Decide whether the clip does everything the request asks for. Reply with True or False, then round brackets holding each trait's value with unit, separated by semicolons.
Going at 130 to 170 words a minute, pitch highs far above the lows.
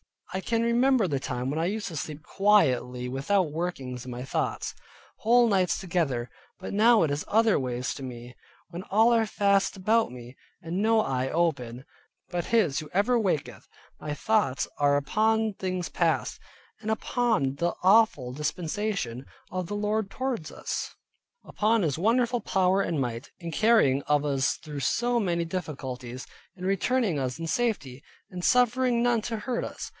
True (165 wpm; 8.0 semitones)